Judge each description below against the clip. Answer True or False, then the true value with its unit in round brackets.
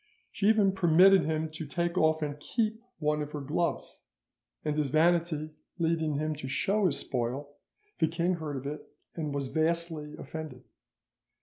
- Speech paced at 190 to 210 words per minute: False (165 wpm)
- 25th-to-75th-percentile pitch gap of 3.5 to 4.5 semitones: False (2.5 semitones)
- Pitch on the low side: False (155 Hz)